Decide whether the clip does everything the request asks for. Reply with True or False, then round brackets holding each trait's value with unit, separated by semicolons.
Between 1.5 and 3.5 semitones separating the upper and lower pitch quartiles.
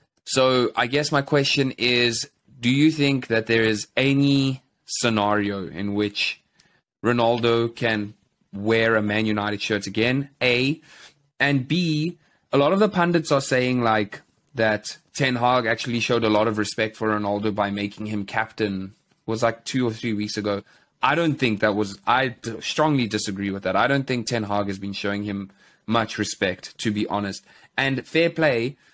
False (4.2 semitones)